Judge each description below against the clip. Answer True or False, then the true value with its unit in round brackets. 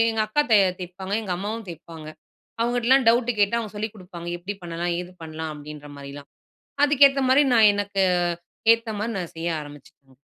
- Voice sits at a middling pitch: False (200 Hz)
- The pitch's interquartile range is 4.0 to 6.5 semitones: True (5.4 semitones)